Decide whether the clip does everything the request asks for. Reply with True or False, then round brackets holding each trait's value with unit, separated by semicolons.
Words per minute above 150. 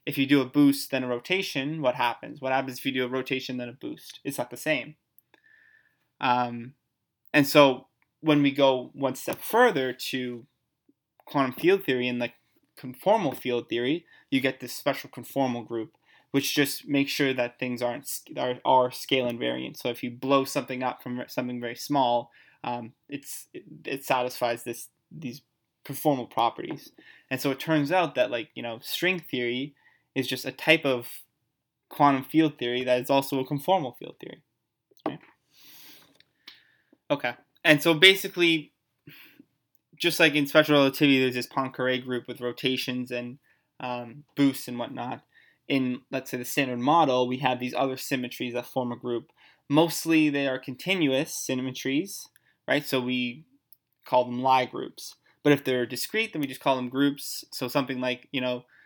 True (170 wpm)